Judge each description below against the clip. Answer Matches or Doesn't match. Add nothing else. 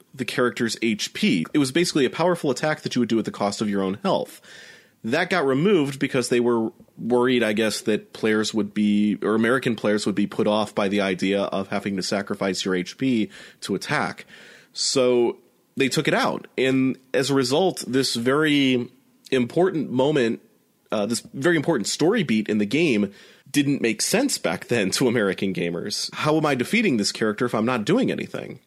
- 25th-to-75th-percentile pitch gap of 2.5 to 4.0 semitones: Doesn't match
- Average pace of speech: Matches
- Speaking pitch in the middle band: Doesn't match